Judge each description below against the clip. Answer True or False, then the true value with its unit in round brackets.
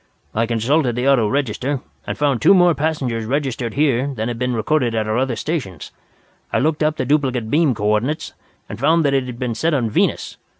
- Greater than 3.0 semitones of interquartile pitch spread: True (4.2 semitones)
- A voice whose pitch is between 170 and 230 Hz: False (130 Hz)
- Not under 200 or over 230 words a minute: True (205 wpm)